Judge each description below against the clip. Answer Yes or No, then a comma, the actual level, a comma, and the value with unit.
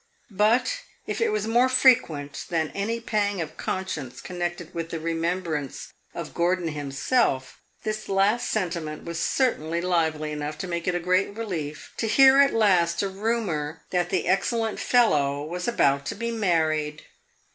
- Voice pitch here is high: No, medium, 175 Hz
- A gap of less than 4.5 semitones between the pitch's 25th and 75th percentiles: No, wide, 5.5 semitones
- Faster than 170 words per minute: No, average, 155 wpm